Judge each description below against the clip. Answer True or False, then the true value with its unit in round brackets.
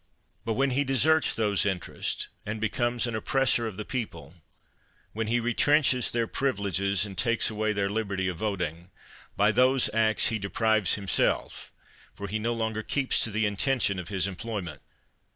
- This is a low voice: True (110 Hz)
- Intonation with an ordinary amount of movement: True (3.2 semitones)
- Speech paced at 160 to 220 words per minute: True (165 wpm)